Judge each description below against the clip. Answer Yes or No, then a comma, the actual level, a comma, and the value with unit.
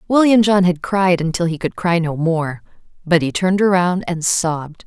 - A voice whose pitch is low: No, medium, 175 Hz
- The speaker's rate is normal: Yes, average, 195 wpm